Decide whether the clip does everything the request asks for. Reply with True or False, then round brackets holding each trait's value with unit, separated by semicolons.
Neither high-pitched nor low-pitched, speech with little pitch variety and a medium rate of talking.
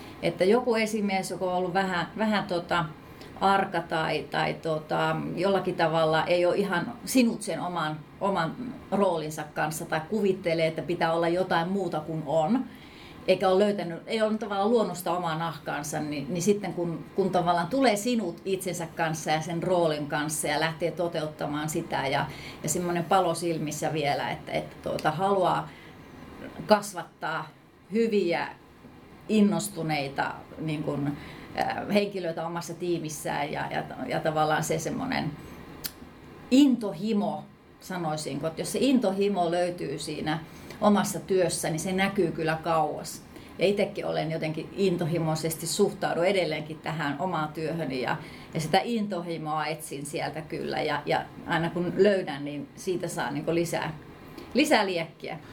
False (170 Hz; 3.4 semitones; 140 wpm)